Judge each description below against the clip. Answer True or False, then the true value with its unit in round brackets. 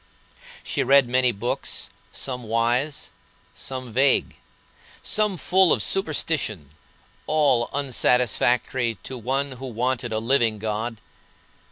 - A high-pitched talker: False (125 Hz)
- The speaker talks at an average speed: False (110 wpm)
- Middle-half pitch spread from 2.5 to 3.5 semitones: True (3.1 semitones)